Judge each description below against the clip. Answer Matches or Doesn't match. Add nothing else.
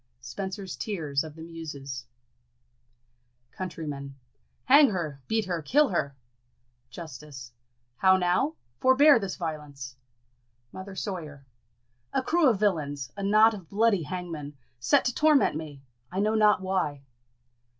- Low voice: Doesn't match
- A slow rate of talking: Matches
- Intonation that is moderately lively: Doesn't match